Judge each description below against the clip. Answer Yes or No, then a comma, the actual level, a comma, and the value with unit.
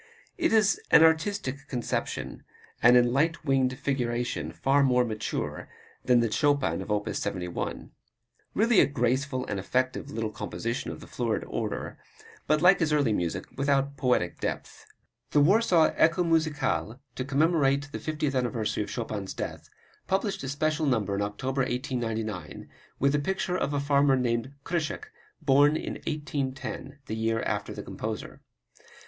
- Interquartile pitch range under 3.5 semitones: No, average, 4.4 semitones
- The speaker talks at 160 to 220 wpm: No, average, 150 wpm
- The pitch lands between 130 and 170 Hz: Yes, low, 135 Hz